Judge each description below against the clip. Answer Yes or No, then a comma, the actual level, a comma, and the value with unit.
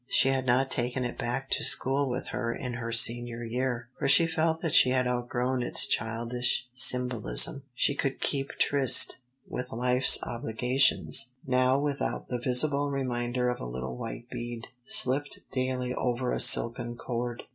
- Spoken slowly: No, average, 160 wpm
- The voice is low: Yes, low, 125 Hz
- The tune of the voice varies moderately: No, narrow, 1.8 semitones